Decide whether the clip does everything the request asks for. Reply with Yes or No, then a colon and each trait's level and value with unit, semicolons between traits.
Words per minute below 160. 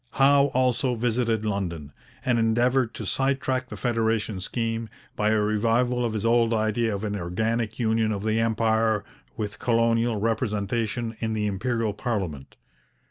Yes: average, 145 wpm